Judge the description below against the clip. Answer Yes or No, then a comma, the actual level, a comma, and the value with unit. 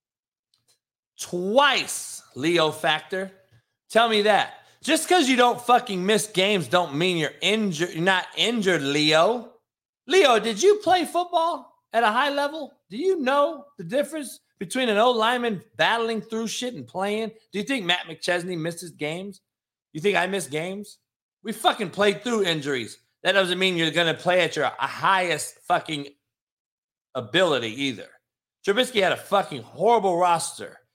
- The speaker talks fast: No, average, 155 wpm